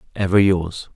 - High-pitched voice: No, very low, 95 Hz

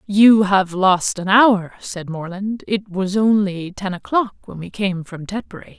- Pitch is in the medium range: No, high, 195 Hz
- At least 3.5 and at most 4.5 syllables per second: Yes, 4.0 syllables/s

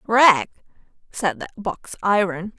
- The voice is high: Yes, high, 205 Hz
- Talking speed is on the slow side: Yes, slow, 115 wpm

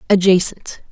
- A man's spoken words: No, female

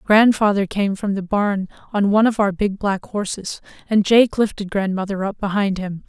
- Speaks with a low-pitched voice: No, high, 200 Hz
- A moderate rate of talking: Yes, average, 190 wpm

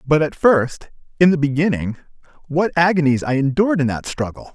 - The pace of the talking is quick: No, average, 170 wpm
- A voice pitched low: No, medium, 150 Hz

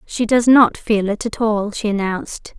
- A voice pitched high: Yes, high, 220 Hz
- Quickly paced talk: Yes, fast, 210 wpm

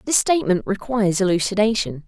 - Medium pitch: No, high, 205 Hz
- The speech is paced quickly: No, slow, 115 wpm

